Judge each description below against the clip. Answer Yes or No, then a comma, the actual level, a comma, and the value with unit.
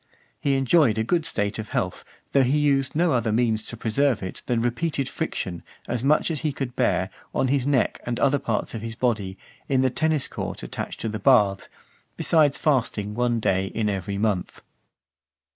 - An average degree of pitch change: Yes, average, 4.5 semitones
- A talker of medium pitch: No, low, 120 Hz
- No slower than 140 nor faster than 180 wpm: No, average, 195 wpm